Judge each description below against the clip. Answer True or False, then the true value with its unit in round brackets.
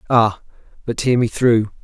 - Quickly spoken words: False (165 wpm)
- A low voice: True (115 Hz)